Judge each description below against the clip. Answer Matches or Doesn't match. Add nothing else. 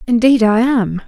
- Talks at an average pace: Matches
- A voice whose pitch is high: Matches